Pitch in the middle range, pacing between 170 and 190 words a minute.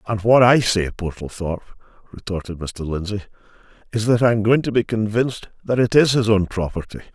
No: low, 105 Hz; average, 175 wpm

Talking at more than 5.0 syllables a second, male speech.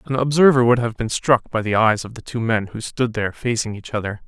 Yes: 5.9 syllables/s; male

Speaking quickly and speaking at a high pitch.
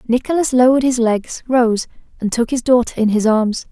No: average, 195 wpm; high, 240 Hz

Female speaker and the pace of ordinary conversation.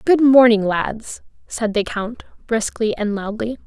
Yes: female; average, 145 wpm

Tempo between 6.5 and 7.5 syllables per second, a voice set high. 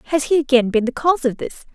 Yes: 7.0 syllables/s; very high, 270 Hz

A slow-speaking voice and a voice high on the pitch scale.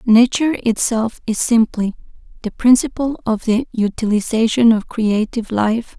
Yes: slow, 120 wpm; high, 225 Hz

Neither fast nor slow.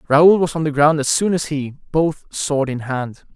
No: fast, 230 wpm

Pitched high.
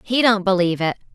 Yes: high, 200 Hz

